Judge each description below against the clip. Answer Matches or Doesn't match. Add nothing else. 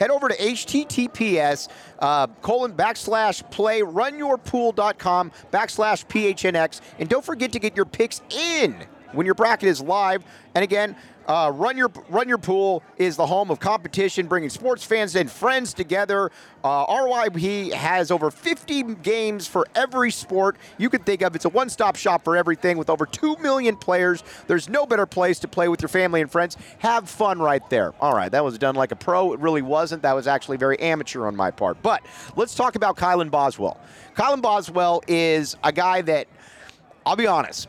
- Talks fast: Doesn't match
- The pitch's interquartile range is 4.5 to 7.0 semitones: Matches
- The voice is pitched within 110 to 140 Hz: Doesn't match